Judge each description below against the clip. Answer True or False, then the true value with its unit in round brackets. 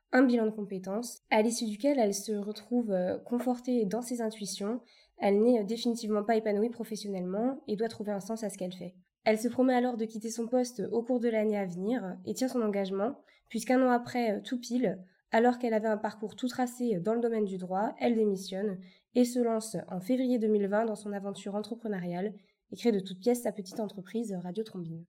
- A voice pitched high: True (220 Hz)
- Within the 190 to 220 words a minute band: True (205 wpm)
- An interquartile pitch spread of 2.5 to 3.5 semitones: True (3.0 semitones)